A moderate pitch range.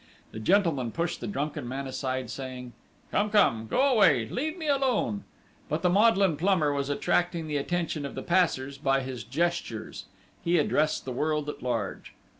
No: wide, 5.7 semitones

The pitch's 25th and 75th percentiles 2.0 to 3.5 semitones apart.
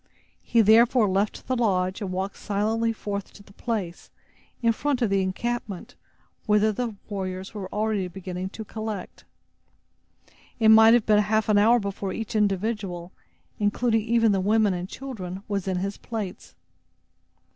Yes: average, 2.7 semitones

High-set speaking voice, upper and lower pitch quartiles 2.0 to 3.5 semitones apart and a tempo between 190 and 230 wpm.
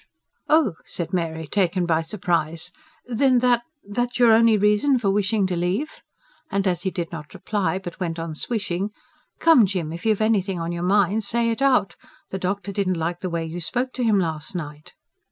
No: high, 195 Hz; average, 4.4 semitones; average, 195 wpm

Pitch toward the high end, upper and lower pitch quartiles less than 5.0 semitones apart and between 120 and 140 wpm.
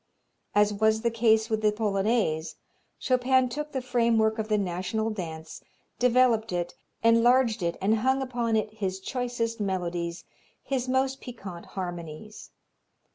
Yes: high, 220 Hz; average, 4.1 semitones; slow, 135 wpm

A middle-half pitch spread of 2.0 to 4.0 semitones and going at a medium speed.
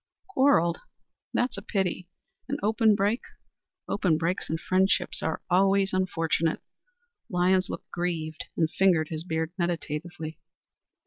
No: average, 3.1 semitones; slow, 125 wpm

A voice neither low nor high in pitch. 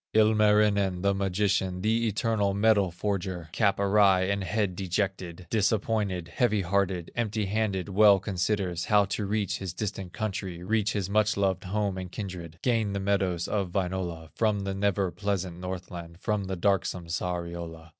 No: low, 100 Hz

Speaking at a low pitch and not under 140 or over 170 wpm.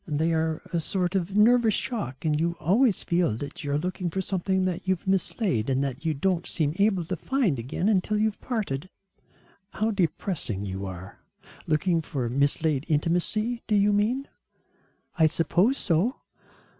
No: medium, 175 Hz; average, 165 wpm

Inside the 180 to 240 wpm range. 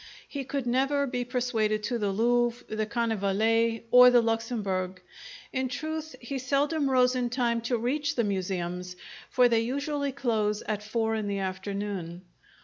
No: average, 155 wpm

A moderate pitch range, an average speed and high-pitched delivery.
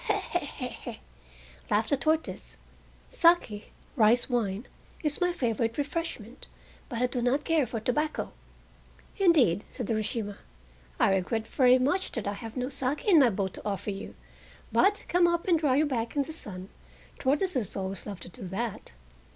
No: wide, 6.1 semitones; average, 165 wpm; high, 245 Hz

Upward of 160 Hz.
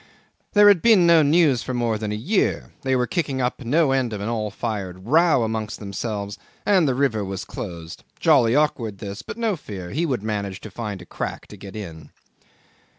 No: low, 115 Hz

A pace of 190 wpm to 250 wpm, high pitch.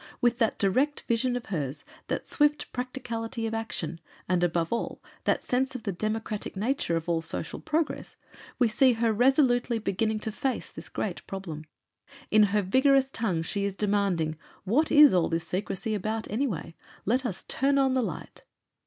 No: average, 170 wpm; high, 220 Hz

